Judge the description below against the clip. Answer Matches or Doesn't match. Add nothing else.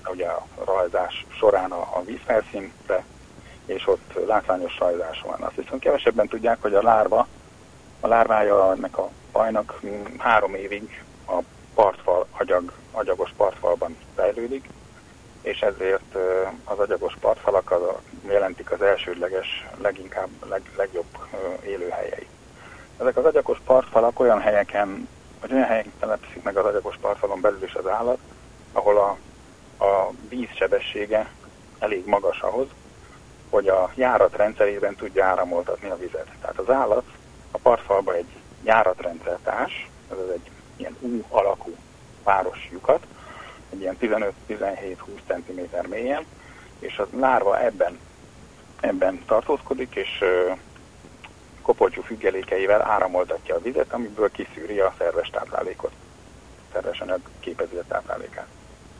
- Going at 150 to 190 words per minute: Doesn't match